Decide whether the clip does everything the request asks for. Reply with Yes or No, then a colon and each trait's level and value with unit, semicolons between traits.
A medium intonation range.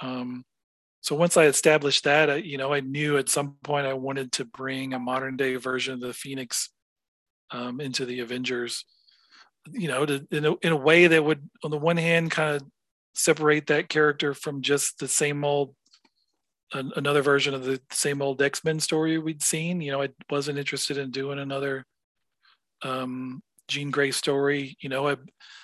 No: narrow, 2.2 semitones